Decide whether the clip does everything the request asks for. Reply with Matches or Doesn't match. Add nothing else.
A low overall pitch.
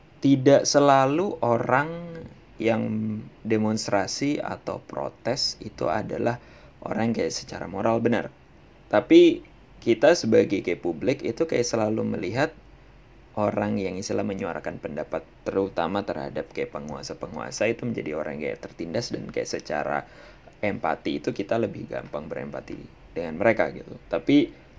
Matches